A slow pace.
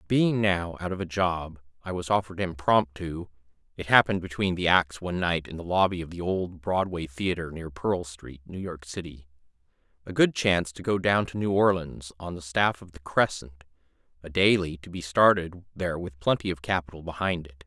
No: average, 195 wpm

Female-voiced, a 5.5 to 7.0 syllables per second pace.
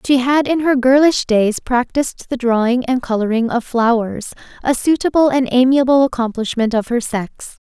No: female; 4.9 syllables/s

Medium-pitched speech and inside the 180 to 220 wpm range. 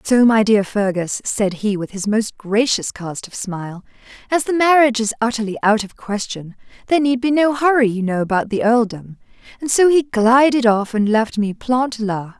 No: high, 225 Hz; average, 200 wpm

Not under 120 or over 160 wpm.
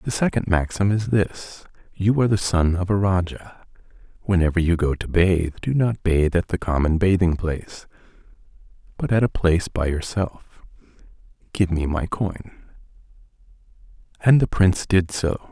Yes: average, 155 wpm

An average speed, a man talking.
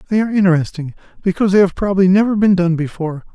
Yes: average, 195 wpm; male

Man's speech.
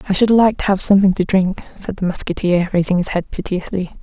No: female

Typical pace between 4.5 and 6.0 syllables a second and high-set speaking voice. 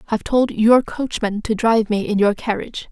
Yes: 5.6 syllables/s; high, 220 Hz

